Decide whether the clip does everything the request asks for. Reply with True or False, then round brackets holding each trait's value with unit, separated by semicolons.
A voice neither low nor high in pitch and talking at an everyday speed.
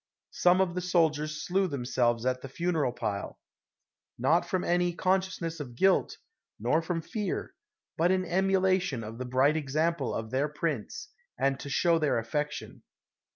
True (160 Hz; 155 wpm)